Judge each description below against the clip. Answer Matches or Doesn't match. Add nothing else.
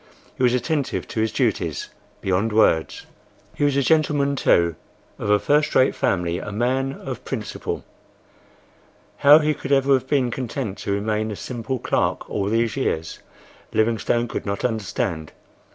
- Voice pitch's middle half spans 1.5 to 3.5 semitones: Doesn't match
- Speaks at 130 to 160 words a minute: Matches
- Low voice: Matches